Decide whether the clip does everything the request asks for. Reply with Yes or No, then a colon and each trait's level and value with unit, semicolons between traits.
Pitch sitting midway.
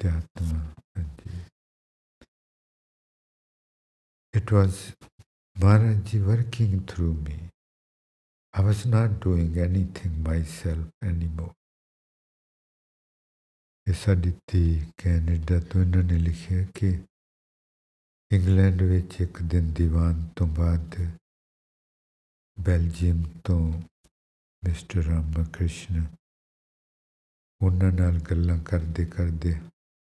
No: very low, 85 Hz